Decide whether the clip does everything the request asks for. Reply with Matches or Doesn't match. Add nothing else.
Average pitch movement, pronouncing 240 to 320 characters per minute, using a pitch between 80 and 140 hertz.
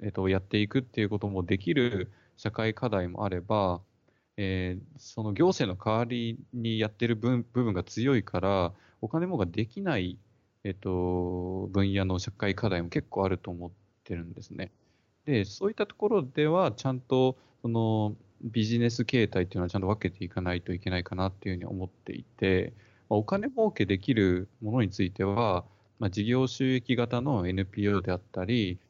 Doesn't match